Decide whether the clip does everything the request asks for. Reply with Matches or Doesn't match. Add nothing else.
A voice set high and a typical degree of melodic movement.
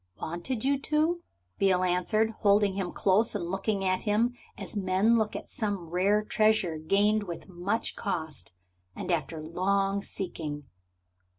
Matches